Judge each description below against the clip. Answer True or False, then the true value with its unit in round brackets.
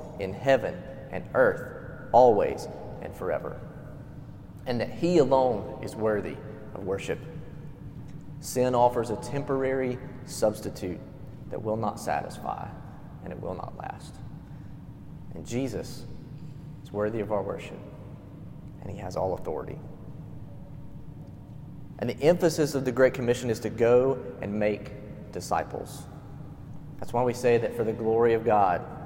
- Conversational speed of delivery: False (130 wpm)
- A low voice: True (125 Hz)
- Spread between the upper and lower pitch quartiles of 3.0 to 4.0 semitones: False (4.6 semitones)